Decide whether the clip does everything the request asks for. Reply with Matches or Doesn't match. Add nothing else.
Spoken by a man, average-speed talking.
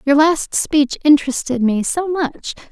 Doesn't match